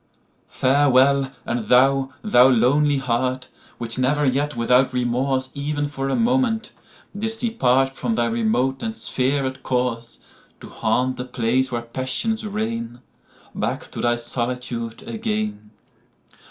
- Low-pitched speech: Yes, low, 130 Hz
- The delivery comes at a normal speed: No, slow, 110 wpm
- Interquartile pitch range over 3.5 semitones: No, average, 3.0 semitones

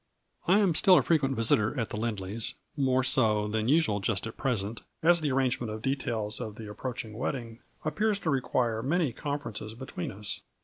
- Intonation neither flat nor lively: Yes, average, 4.7 semitones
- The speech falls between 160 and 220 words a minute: Yes, average, 195 wpm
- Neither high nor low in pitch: No, low, 120 Hz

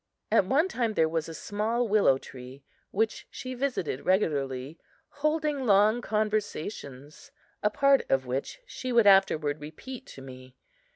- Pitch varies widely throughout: Yes, wide, 9.0 semitones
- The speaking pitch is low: No, high, 205 Hz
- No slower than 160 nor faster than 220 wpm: No, average, 140 wpm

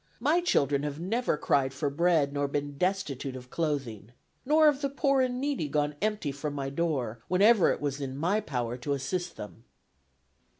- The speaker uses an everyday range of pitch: No, wide, 7.0 semitones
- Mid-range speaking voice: Yes, medium, 150 Hz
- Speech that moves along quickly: No, average, 180 wpm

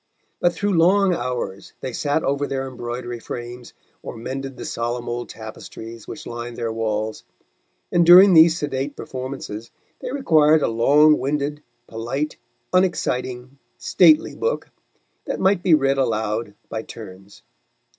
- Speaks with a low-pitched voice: Yes, low, 130 Hz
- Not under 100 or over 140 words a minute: Yes, slow, 135 wpm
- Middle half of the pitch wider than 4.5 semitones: Yes, average, 4.9 semitones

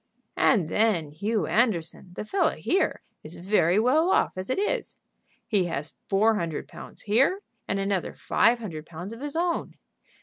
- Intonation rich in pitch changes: Yes, wide, 5.9 semitones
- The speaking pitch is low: No, high, 205 Hz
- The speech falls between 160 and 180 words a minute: Yes, average, 165 wpm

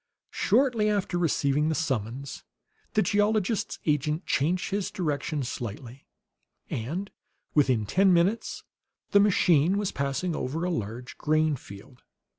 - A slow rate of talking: Yes, slow, 120 wpm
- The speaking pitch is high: No, medium, 155 Hz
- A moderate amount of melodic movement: No, wide, 6.2 semitones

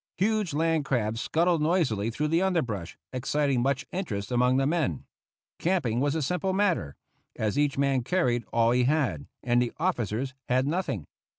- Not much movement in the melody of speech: No, wide, 5.6 semitones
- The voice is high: No, medium, 140 Hz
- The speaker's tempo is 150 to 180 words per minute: Yes, average, 165 wpm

